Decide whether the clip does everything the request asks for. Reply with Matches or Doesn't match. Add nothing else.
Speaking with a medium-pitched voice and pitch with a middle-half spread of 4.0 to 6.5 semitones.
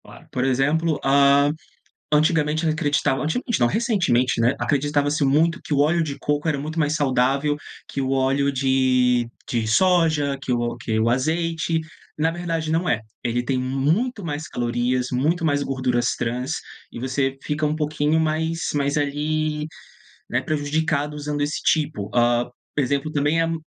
Doesn't match